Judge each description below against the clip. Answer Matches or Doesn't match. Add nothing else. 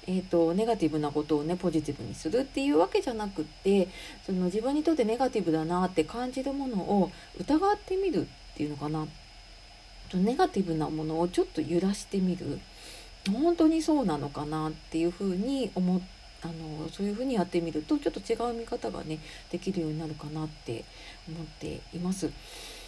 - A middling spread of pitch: Doesn't match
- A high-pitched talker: Doesn't match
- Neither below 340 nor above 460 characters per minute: Matches